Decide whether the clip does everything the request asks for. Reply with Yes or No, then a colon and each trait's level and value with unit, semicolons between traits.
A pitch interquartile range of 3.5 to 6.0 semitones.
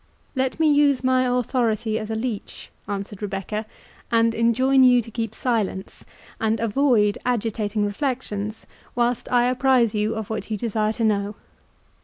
No: average, 2.9 semitones